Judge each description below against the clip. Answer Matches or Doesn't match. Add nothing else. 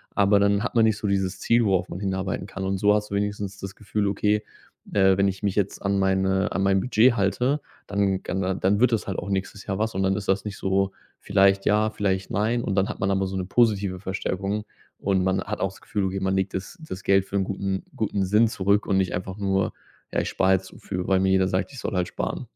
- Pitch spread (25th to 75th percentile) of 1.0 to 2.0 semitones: Matches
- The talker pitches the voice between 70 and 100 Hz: Matches